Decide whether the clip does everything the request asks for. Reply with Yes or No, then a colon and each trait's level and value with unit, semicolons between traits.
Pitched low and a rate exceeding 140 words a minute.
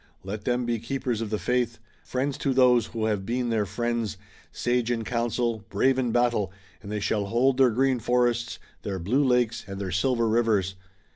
Yes: low, 120 Hz; average, 190 wpm